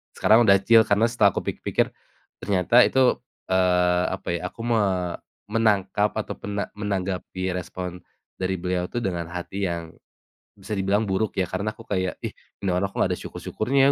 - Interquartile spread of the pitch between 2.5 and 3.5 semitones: Yes, average, 2.9 semitones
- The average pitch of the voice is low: Yes, low, 100 Hz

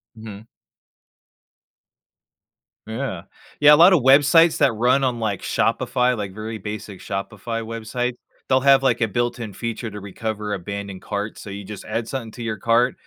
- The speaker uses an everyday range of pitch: Yes, average, 3.3 semitones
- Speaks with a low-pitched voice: Yes, low, 115 Hz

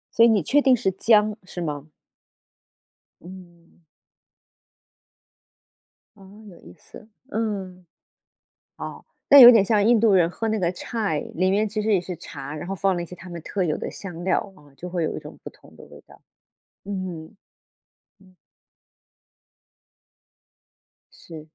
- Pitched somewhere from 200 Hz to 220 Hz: No, high, 190 Hz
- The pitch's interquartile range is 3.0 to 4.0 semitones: Yes, average, 3.6 semitones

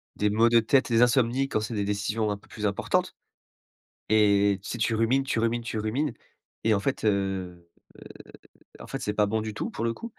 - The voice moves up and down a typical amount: No, narrow, 2.3 semitones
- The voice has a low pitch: Yes, low, 110 Hz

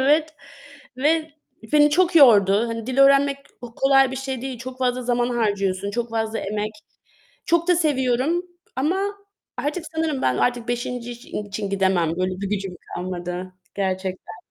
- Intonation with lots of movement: Yes, wide, 5.8 semitones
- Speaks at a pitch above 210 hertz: Yes, high, 245 Hz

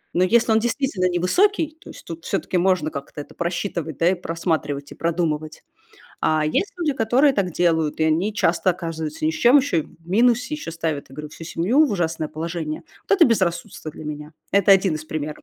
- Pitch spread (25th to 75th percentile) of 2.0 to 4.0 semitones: No, average, 5.1 semitones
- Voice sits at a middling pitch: Yes, medium, 170 Hz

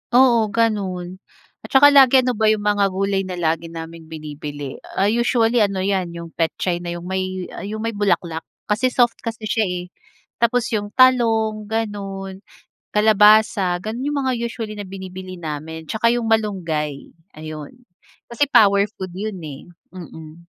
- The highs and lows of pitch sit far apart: No, average, 4.3 semitones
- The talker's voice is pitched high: Yes, high, 200 Hz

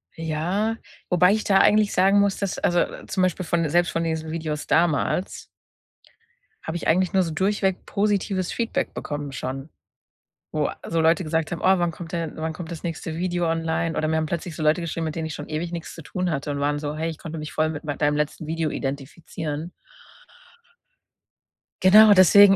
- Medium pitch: Yes, medium, 165 Hz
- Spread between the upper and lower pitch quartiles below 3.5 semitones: Yes, average, 2.8 semitones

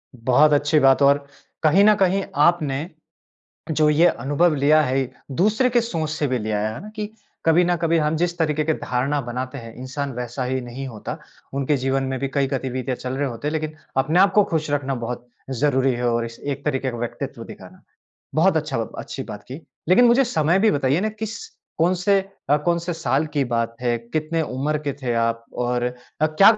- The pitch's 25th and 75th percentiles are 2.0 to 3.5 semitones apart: No, average, 4.2 semitones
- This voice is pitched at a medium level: Yes, medium, 145 Hz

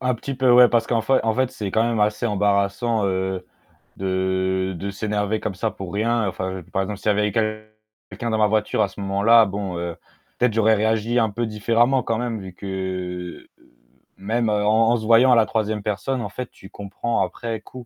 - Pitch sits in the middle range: No, low, 110 Hz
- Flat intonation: No, average, 3.0 semitones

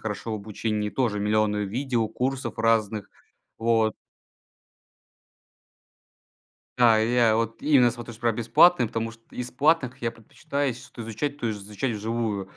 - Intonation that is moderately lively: No, narrow, 2.3 semitones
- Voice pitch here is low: Yes, low, 115 Hz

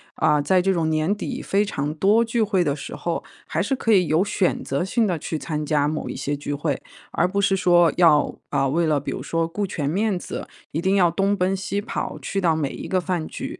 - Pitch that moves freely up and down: No, average, 4.2 semitones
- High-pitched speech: No, medium, 175 Hz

